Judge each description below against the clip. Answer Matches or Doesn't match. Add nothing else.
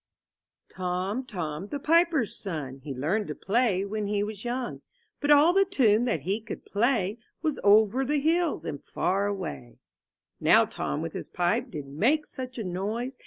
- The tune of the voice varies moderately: Doesn't match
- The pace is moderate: Matches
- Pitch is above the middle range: Matches